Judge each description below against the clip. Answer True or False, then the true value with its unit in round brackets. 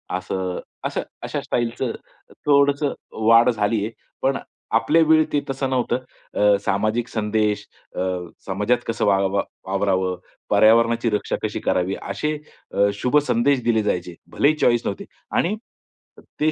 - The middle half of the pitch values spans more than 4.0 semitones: True (4.4 semitones)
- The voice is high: False (115 Hz)